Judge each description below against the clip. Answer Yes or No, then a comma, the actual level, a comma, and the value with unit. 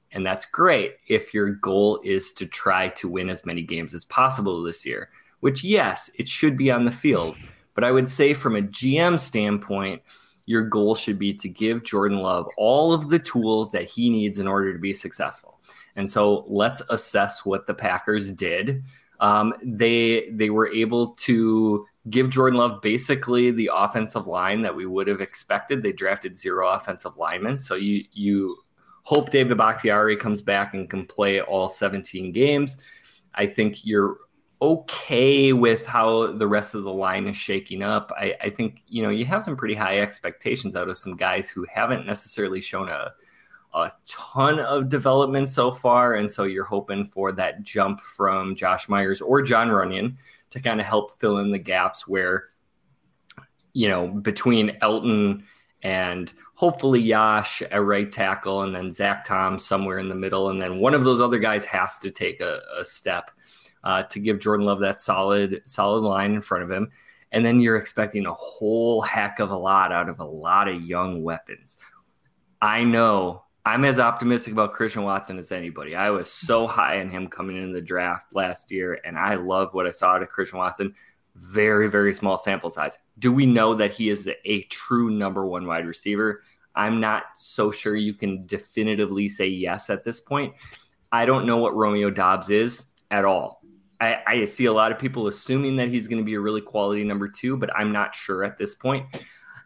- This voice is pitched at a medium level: No, low, 105 Hz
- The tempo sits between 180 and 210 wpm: Yes, average, 190 wpm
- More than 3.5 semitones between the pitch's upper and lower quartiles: No, average, 3.2 semitones